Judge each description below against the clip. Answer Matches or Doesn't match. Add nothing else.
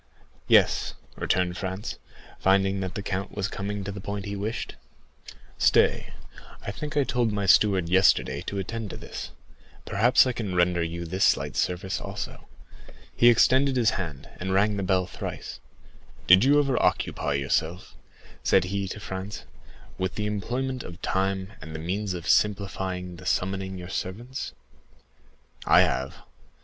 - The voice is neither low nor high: Doesn't match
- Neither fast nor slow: Matches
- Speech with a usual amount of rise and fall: Doesn't match